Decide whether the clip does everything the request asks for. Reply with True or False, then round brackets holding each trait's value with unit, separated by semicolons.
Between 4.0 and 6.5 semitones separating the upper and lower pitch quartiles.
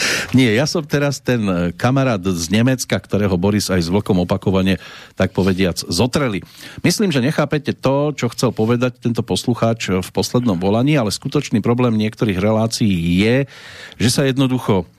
True (5.0 semitones)